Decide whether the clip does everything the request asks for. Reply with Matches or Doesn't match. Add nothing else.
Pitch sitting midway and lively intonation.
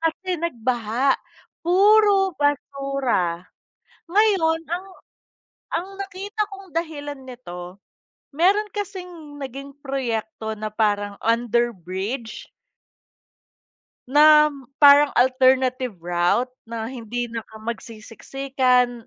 Doesn't match